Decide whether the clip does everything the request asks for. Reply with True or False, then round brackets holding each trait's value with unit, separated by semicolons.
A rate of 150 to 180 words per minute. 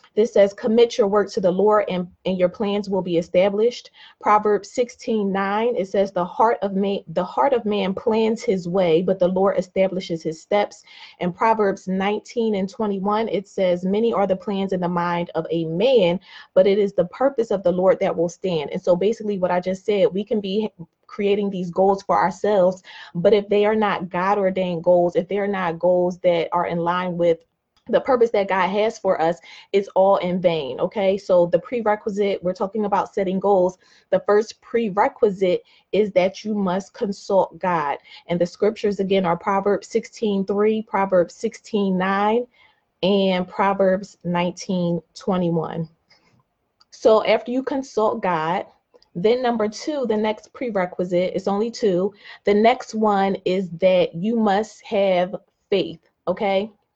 True (175 wpm)